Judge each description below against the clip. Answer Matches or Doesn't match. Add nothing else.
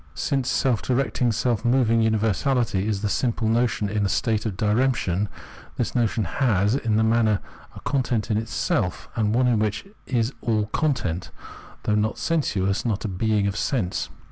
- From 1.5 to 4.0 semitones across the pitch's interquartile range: Matches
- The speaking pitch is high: Doesn't match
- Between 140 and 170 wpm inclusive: Matches